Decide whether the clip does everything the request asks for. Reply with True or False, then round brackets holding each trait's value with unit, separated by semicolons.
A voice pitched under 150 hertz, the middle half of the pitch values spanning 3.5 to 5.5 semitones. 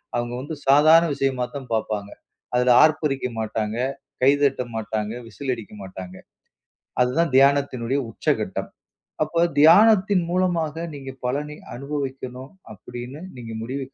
True (135 Hz; 3.8 semitones)